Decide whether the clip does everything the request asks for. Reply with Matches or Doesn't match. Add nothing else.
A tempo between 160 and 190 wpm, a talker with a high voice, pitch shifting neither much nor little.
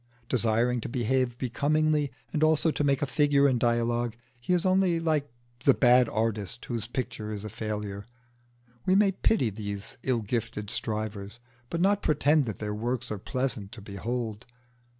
Doesn't match